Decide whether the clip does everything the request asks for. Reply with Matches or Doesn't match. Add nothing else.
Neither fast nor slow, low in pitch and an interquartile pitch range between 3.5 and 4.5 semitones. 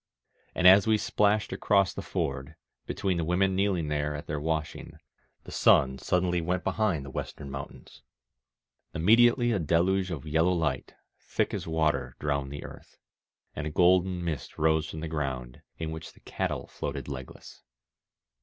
Matches